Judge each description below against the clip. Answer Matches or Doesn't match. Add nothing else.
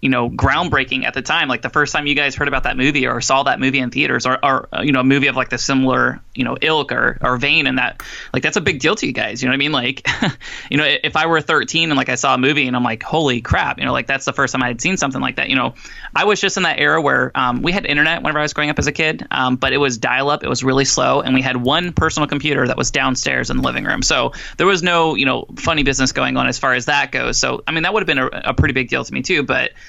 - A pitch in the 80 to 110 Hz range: Doesn't match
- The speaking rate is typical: Doesn't match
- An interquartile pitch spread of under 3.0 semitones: Matches